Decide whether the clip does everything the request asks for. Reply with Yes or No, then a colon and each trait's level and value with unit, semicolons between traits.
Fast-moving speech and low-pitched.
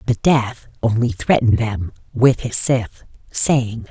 No: average, 140 wpm; low, 115 Hz